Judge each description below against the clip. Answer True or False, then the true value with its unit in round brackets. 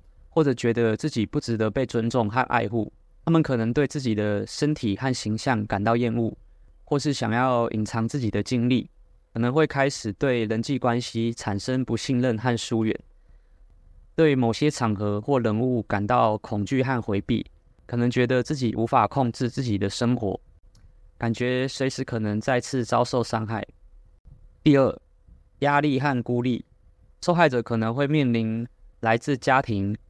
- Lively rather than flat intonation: False (3.4 semitones)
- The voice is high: False (115 Hz)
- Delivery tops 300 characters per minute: False (245 characters per minute)